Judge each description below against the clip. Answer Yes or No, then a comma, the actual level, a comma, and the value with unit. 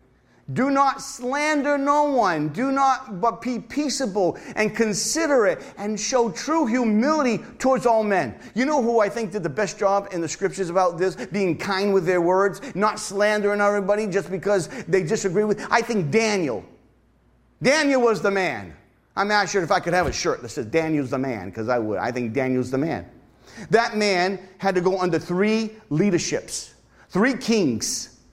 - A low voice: No, high, 205 Hz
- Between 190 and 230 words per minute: No, average, 180 wpm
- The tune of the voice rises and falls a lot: No, average, 4.4 semitones